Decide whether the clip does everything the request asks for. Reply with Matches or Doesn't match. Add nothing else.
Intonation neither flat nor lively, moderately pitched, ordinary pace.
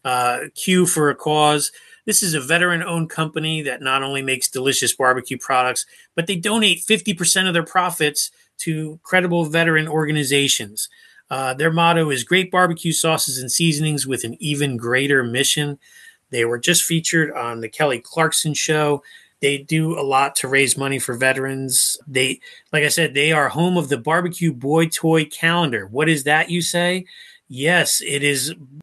Matches